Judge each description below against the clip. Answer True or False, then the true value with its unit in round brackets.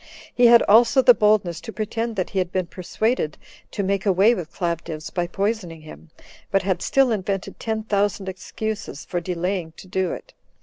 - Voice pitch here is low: False (195 Hz)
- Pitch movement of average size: True (3.7 semitones)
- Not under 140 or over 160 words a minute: False (180 wpm)